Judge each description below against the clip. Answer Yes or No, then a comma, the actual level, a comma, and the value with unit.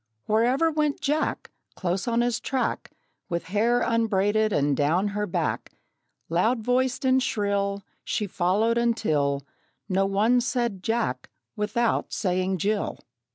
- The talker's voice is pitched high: Yes, high, 215 Hz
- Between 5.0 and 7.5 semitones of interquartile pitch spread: No, average, 4.0 semitones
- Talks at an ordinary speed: No, slow, 125 wpm